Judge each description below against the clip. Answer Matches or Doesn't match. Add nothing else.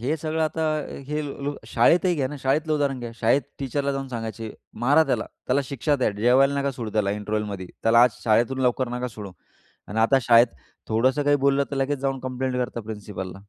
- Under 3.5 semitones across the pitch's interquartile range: Doesn't match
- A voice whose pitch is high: Doesn't match